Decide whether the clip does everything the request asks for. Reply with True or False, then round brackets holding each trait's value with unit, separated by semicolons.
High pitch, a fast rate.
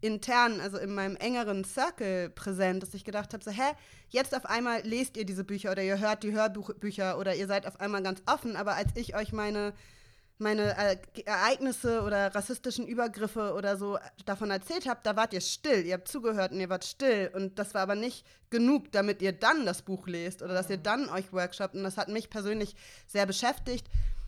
True (205 Hz; 205 wpm)